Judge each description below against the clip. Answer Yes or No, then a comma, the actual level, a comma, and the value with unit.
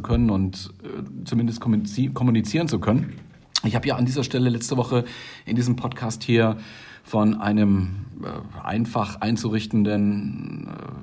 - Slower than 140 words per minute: Yes, average, 130 wpm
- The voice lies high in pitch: No, low, 115 Hz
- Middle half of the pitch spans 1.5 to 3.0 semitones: Yes, narrow, 2.6 semitones